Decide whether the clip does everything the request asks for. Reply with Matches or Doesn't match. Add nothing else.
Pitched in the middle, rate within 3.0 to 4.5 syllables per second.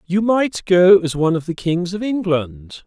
Matches